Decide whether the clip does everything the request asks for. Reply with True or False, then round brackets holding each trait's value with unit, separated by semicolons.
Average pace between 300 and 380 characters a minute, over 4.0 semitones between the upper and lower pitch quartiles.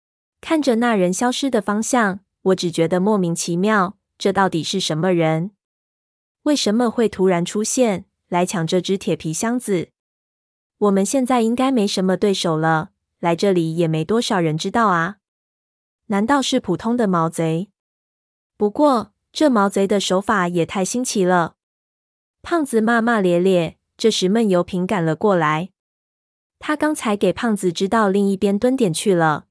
False (230 characters per minute; 4.5 semitones)